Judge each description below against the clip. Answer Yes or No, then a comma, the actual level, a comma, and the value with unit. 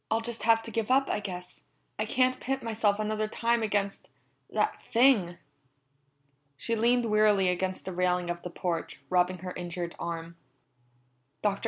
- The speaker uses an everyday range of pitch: Yes, average, 4.1 semitones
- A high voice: Yes, high, 205 Hz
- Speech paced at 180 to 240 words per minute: No, average, 160 wpm